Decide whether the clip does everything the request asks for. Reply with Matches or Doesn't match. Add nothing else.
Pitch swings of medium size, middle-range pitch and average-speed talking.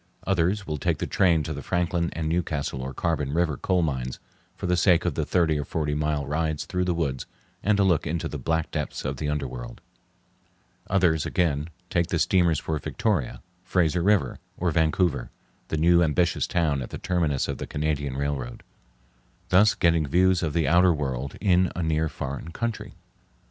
Doesn't match